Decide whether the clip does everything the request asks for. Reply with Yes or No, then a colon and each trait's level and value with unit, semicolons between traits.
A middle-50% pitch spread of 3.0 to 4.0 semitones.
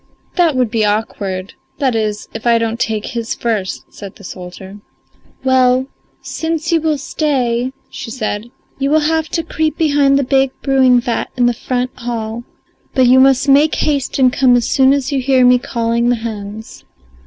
Yes: average, 3.4 semitones